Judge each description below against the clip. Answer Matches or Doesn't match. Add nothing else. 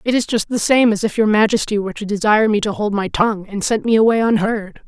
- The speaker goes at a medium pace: Doesn't match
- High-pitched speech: Matches